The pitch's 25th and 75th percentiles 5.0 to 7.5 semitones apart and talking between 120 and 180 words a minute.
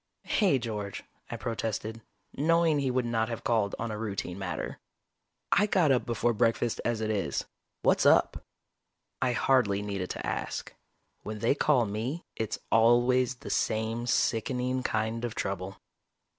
No: average, 2.9 semitones; average, 150 wpm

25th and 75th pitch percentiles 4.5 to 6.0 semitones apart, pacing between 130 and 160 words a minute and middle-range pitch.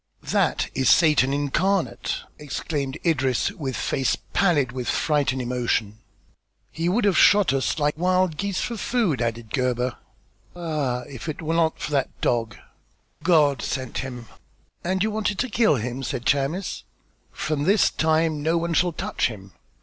Yes: average, 5.3 semitones; average, 155 wpm; medium, 150 Hz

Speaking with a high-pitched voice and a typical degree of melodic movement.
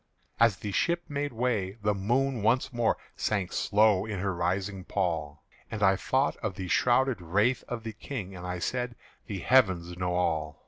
No: low, 105 Hz; average, 4.9 semitones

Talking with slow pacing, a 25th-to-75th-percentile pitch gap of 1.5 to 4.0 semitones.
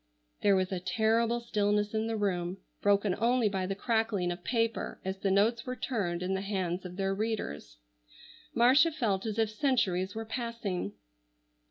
No: average, 170 wpm; average, 3.3 semitones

